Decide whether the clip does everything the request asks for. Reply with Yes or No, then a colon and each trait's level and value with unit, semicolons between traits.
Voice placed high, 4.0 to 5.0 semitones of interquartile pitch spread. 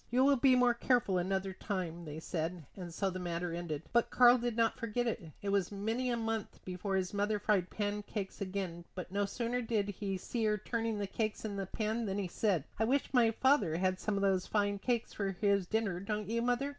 No: high, 205 Hz; average, 3.6 semitones